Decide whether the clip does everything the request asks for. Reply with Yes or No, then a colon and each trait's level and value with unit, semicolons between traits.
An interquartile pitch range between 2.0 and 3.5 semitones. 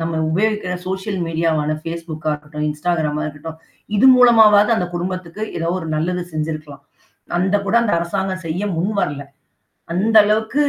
No: average, 4.1 semitones